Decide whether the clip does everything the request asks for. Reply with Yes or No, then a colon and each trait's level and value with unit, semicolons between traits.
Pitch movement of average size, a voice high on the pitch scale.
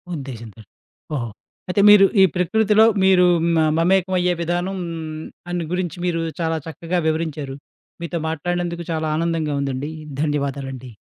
No: average, 3.4 semitones; medium, 165 Hz